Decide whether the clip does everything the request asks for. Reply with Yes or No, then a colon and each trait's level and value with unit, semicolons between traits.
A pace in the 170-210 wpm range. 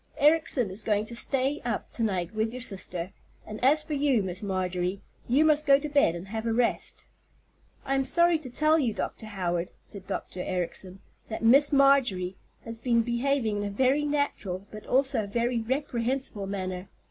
Yes: average, 185 wpm